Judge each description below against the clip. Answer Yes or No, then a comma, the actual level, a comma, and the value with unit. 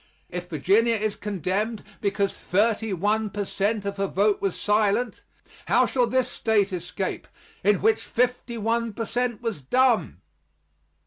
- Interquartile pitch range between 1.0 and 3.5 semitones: Yes, average, 2.7 semitones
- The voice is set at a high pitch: Yes, high, 210 Hz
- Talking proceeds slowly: No, average, 145 wpm